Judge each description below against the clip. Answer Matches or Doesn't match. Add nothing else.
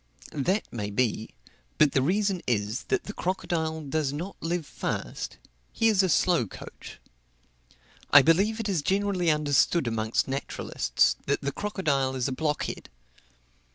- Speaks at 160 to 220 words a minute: Doesn't match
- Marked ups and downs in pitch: Matches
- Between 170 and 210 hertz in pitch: Doesn't match